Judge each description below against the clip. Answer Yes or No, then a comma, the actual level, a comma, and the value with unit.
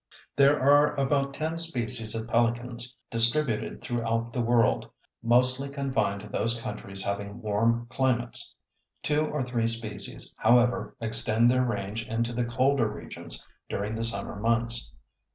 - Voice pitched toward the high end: No, low, 120 Hz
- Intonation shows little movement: Yes, narrow, 2.3 semitones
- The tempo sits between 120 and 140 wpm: Yes, slow, 135 wpm